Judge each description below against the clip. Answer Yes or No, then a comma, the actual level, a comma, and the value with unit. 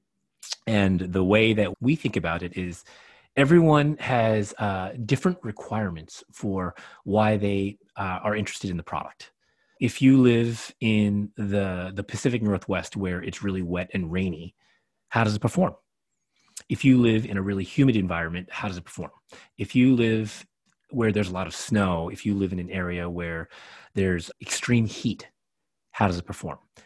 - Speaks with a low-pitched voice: Yes, low, 100 Hz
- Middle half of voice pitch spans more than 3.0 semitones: Yes, average, 3.5 semitones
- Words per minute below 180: Yes, average, 170 wpm